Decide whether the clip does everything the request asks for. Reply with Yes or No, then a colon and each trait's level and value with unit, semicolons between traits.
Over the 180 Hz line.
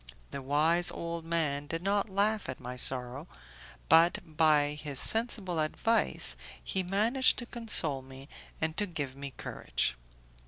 No: medium, 160 Hz